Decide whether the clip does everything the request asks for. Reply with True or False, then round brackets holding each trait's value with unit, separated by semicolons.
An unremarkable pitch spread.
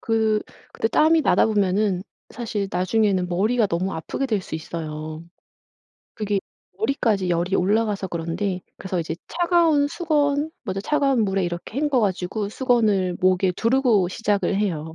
True (4.8 semitones)